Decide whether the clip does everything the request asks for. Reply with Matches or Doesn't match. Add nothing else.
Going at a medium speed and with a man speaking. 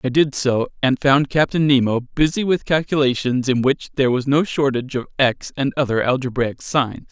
Matches